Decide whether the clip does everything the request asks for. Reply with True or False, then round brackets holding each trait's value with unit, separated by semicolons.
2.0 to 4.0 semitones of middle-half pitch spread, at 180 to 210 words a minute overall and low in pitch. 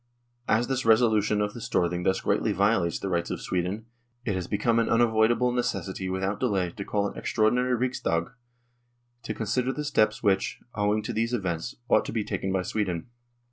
True (3.6 semitones; 185 wpm; 105 Hz)